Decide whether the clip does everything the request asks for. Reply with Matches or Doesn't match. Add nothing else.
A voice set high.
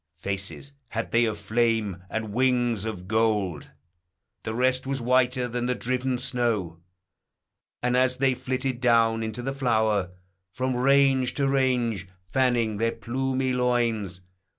Doesn't match